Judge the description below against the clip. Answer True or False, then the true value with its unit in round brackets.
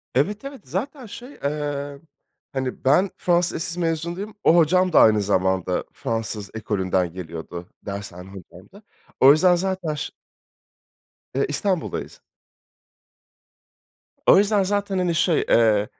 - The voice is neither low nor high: True (150 Hz)